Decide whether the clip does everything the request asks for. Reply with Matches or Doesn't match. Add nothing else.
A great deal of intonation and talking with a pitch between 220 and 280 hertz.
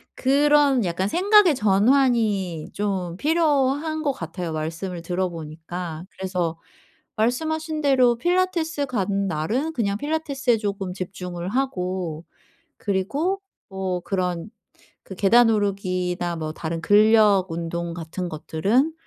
Doesn't match